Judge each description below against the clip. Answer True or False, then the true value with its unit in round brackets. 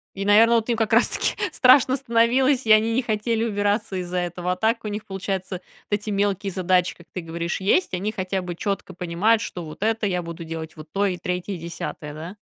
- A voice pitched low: False (195 Hz)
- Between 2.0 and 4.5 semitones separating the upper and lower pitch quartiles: True (3.9 semitones)